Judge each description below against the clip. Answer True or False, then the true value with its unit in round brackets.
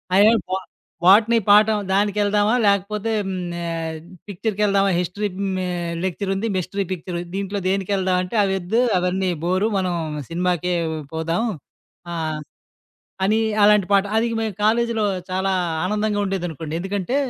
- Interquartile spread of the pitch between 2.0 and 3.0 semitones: True (2.5 semitones)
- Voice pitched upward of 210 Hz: False (195 Hz)